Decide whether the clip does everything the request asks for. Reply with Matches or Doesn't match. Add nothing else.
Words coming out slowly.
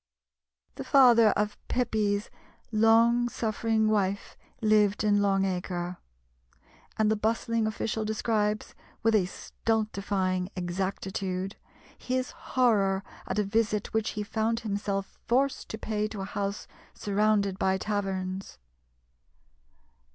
Matches